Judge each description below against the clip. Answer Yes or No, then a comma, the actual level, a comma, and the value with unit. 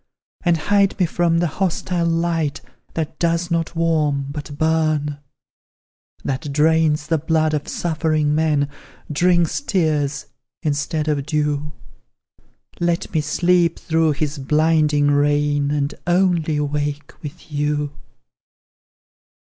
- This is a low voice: No, medium, 155 Hz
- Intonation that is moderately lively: No, narrow, 2.2 semitones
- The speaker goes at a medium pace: No, slow, 115 wpm